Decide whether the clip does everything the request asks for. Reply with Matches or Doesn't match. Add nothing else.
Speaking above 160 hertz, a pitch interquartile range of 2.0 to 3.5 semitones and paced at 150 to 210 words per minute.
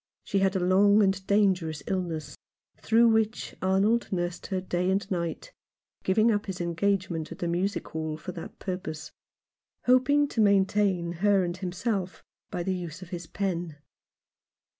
Matches